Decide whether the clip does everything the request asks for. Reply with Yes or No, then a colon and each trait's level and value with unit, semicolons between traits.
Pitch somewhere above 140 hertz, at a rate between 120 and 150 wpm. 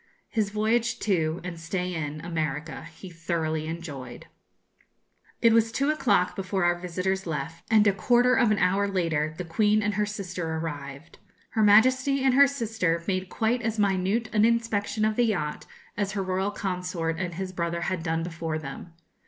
No: medium, 185 Hz; average, 175 wpm